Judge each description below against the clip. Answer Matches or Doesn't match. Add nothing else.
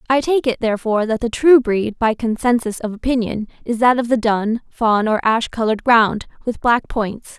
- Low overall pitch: Doesn't match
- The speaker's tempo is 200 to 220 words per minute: Matches